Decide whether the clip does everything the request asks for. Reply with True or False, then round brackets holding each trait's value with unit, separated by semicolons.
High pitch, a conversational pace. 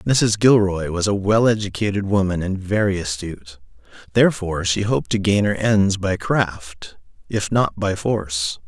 False (100 Hz; 160 wpm)